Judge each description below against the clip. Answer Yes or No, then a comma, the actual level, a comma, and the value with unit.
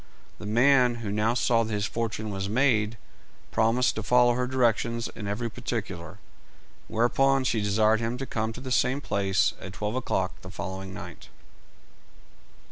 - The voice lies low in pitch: Yes, low, 115 Hz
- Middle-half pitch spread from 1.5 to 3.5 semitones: Yes, average, 3.1 semitones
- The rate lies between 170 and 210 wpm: No, average, 160 wpm